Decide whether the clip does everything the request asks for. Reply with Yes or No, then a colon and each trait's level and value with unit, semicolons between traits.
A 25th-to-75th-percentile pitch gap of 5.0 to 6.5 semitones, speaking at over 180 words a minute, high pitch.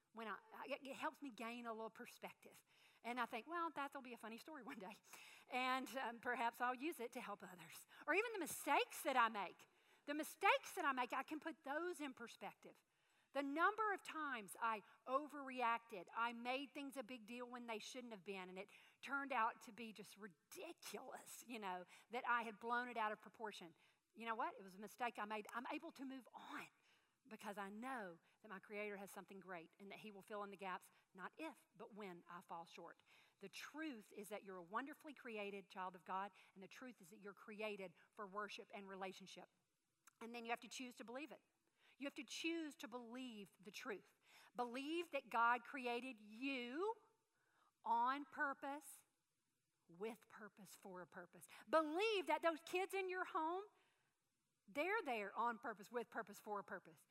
Yes: wide, 5.5 semitones; average, 195 wpm; high, 235 Hz